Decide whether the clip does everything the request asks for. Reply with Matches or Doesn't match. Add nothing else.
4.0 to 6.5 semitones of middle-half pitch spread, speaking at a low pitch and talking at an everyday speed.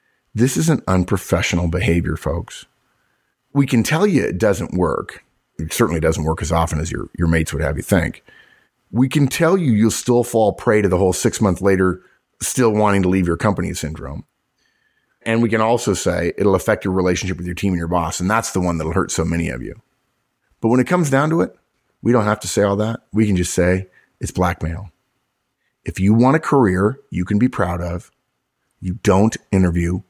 Doesn't match